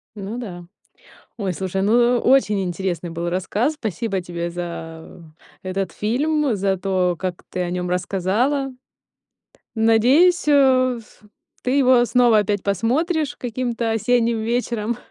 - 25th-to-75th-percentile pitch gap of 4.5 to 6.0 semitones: Yes, average, 5.1 semitones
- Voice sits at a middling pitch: No, high, 220 Hz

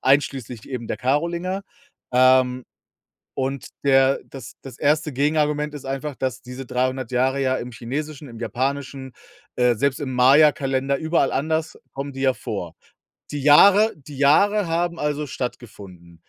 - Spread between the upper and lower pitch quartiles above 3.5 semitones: No, average, 2.7 semitones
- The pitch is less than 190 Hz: Yes, low, 135 Hz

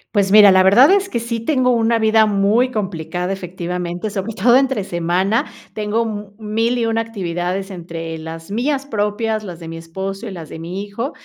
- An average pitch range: Yes, average, 4.2 semitones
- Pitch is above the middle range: Yes, high, 205 Hz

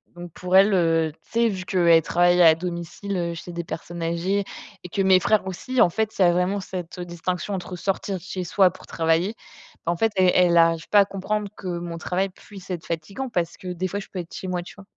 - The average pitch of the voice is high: No, medium, 180 Hz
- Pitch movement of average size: No, narrow, 2.2 semitones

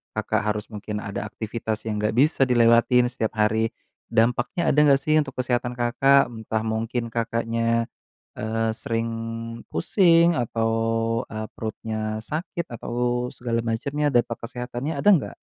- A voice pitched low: Yes, low, 115 Hz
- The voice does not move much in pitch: No, average, 3.3 semitones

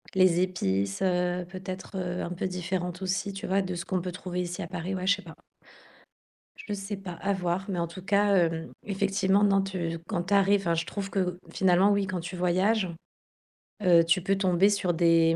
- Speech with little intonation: Yes, narrow, 1.9 semitones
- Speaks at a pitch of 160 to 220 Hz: Yes, medium, 185 Hz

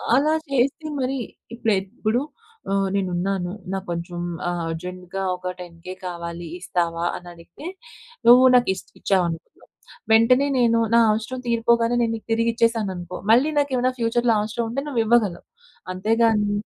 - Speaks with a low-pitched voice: No, high, 215 Hz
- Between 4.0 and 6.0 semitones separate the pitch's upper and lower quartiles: Yes, average, 4.7 semitones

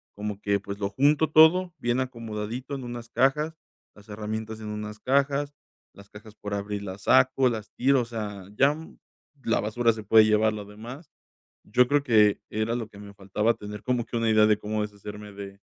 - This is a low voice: Yes, low, 110 Hz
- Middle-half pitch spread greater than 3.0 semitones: Yes, average, 3.5 semitones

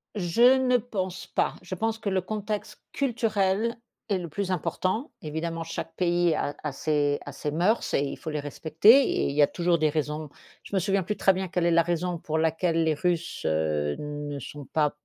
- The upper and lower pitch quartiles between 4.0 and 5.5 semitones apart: Yes, average, 4.4 semitones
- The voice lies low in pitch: No, medium, 170 Hz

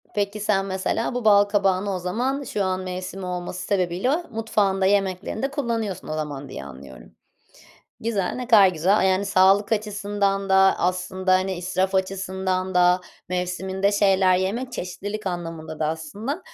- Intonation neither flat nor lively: No, narrow, 2.1 semitones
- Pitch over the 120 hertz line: Yes, high, 190 Hz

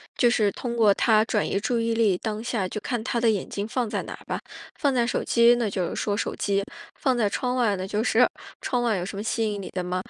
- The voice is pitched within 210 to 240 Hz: Yes, high, 220 Hz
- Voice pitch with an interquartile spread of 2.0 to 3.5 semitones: Yes, average, 2.9 semitones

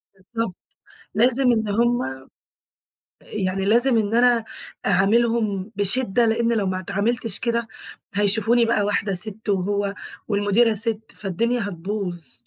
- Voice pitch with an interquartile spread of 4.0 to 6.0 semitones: No, average, 2.9 semitones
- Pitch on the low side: No, high, 215 Hz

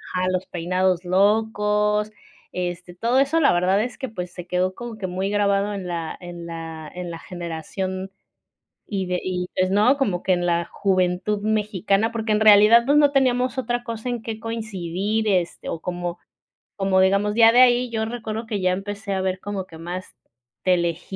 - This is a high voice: Yes, high, 195 Hz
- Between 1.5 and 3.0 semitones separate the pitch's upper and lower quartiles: No, average, 3.5 semitones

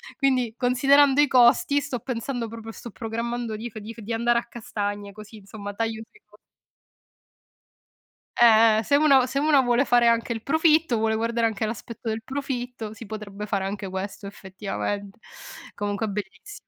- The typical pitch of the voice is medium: No, high, 230 Hz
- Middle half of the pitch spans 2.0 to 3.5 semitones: Yes, average, 2.9 semitones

